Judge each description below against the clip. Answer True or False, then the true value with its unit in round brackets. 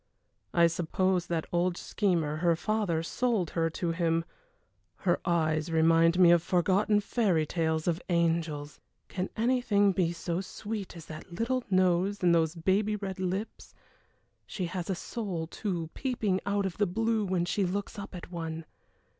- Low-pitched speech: False (180 Hz)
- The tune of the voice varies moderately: True (3.3 semitones)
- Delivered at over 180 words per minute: False (160 wpm)